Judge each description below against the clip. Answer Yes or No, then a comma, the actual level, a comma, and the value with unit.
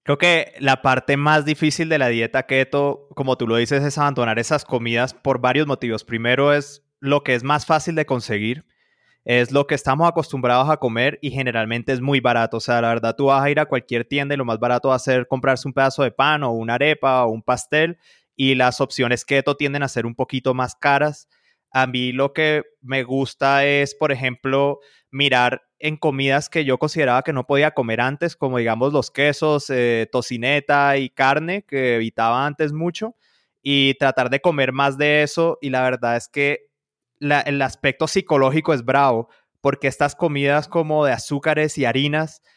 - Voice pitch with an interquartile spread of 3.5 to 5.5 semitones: No, narrow, 2.6 semitones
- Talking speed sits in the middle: No, fast, 195 wpm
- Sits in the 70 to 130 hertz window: No, medium, 140 Hz